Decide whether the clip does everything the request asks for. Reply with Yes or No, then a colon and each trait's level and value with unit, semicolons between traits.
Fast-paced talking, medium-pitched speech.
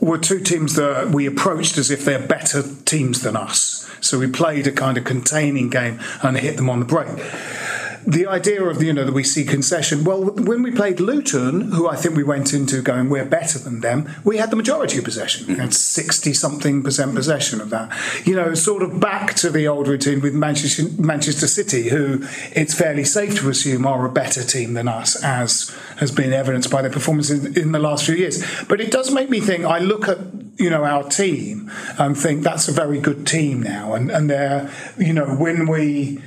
Yes: fast, 215 wpm; medium, 150 Hz